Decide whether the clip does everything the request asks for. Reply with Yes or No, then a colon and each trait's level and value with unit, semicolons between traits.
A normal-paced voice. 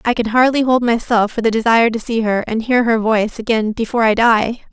No: fast, 240 wpm